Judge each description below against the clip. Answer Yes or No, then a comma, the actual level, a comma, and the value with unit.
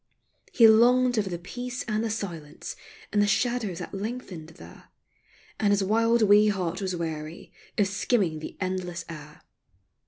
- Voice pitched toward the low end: No, high, 200 Hz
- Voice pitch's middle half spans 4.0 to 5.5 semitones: Yes, average, 4.8 semitones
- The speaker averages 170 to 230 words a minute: No, average, 155 wpm